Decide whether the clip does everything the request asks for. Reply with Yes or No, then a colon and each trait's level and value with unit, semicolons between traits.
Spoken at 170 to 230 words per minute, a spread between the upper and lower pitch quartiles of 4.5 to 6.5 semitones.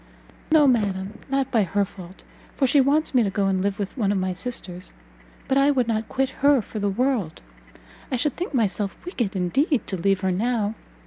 Yes: fast, 205 wpm; wide, 5.5 semitones